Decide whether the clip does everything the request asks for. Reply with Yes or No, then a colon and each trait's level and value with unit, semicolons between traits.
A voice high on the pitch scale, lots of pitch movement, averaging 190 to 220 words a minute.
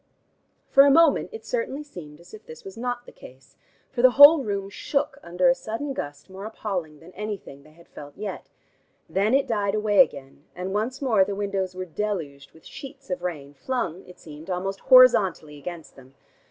Yes: high, 195 Hz; wide, 7.0 semitones; average, 195 wpm